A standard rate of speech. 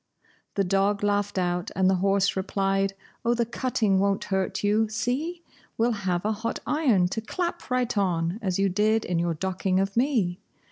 Yes: average, 180 wpm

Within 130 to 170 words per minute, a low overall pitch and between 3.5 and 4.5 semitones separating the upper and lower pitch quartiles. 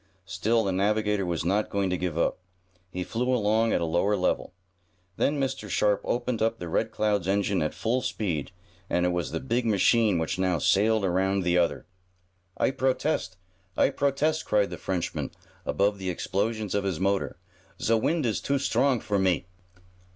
No: average, 180 wpm; low, 100 Hz; average, 3.8 semitones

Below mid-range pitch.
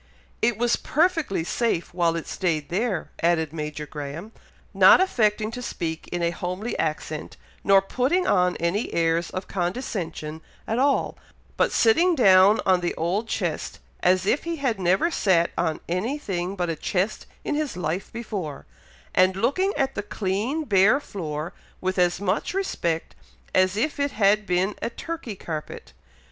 No: high, 190 Hz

